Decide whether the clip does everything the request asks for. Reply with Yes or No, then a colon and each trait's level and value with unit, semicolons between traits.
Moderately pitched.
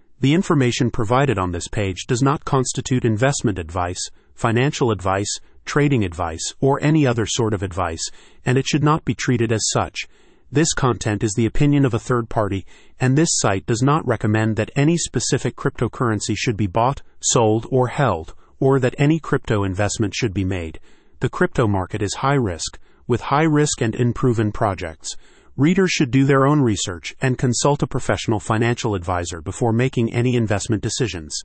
No: low, 120 Hz